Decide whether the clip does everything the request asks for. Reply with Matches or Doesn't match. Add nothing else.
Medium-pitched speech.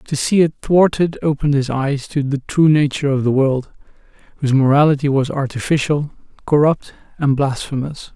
Matches